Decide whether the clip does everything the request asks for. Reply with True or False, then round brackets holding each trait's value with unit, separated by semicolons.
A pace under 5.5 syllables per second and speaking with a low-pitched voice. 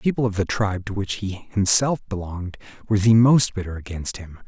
False (6.0 syllables/s; 100 Hz)